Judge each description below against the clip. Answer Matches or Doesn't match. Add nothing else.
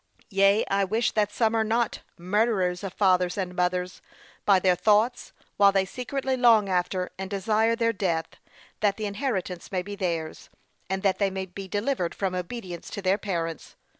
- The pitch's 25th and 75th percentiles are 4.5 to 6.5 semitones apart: Doesn't match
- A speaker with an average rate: Matches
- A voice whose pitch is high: Matches